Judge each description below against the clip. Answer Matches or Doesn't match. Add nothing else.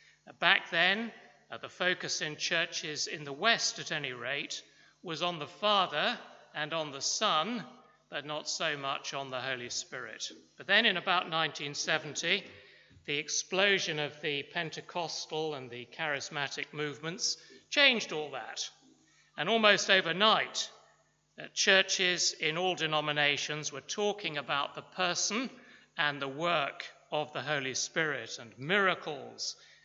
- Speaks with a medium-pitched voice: Matches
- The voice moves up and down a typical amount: Matches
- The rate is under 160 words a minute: Matches